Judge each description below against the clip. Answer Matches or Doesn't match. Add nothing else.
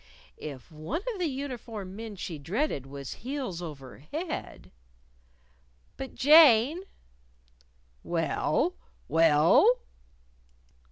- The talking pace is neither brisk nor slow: Doesn't match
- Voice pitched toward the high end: Matches